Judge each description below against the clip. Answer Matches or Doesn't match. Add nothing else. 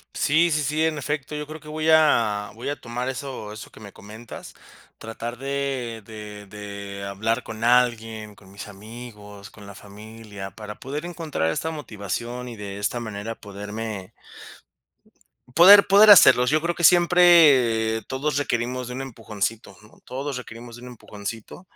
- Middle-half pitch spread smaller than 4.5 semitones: Doesn't match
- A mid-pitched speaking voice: Doesn't match